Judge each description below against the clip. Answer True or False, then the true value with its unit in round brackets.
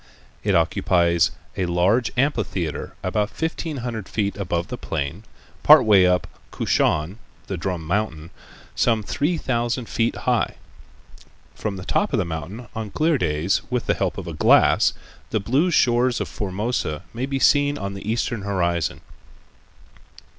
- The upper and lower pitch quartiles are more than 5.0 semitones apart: True (5.4 semitones)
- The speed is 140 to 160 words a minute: True (150 wpm)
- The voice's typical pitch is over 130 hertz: False (105 Hz)